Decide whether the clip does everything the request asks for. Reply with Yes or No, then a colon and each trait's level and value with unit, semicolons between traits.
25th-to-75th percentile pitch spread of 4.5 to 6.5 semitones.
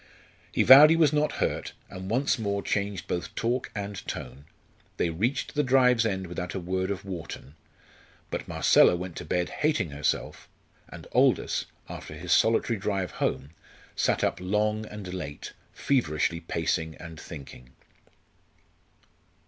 Yes: average, 5.1 semitones